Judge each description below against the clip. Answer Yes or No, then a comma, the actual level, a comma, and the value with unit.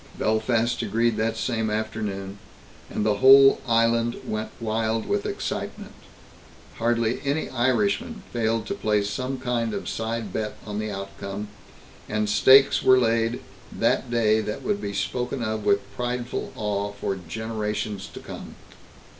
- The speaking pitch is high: No, low, 110 Hz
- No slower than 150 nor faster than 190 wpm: No, average, 140 wpm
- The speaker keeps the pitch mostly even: Yes, narrow, 2.3 semitones